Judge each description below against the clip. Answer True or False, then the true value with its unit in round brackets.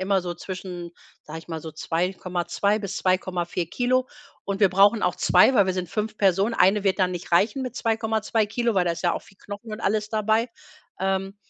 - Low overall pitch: False (195 Hz)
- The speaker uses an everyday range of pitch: True (3.2 semitones)